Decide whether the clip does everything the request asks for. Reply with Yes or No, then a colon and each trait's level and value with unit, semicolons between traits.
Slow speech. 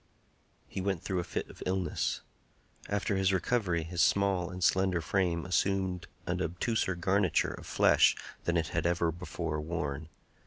No: average, 155 wpm